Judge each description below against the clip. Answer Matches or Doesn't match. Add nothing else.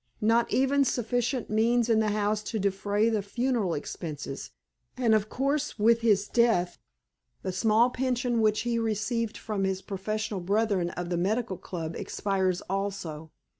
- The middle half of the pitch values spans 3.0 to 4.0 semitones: Matches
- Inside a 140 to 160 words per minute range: Matches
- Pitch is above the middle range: Matches